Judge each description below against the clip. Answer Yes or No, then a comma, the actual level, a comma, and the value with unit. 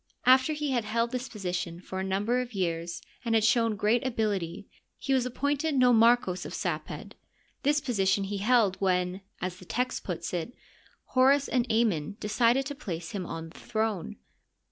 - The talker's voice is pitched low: No, high, 220 Hz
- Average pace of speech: Yes, average, 170 wpm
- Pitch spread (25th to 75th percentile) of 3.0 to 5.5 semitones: Yes, average, 5.2 semitones